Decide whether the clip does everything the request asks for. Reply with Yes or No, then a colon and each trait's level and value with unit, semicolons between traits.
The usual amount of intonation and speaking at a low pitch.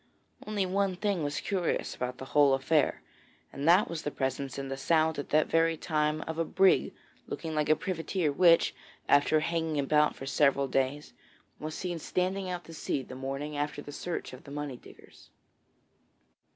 No: average, 3.2 semitones; medium, 155 Hz